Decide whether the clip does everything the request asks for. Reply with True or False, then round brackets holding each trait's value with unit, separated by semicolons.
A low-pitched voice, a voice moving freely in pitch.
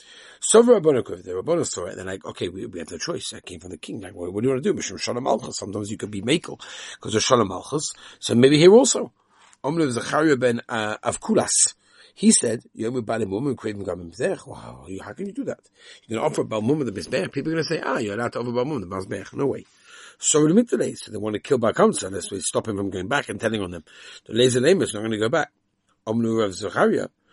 True (120 Hz; 6.9 semitones)